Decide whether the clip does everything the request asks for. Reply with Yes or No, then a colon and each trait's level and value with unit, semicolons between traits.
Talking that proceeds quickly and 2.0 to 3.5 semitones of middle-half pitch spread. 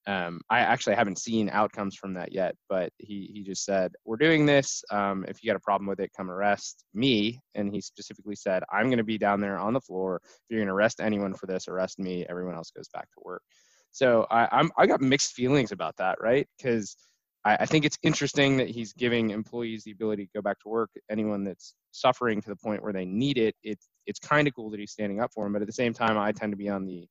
Yes: fast, 250 wpm; average, 2.8 semitones